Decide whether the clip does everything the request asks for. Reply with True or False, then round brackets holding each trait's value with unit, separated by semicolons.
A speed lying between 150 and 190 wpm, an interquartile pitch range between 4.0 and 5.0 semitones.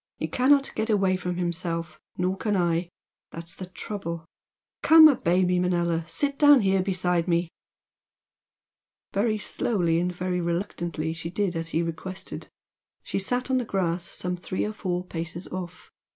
False (155 wpm; 2.7 semitones)